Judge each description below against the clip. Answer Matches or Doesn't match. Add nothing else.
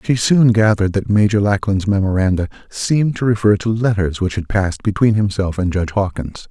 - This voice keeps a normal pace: Matches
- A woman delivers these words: Doesn't match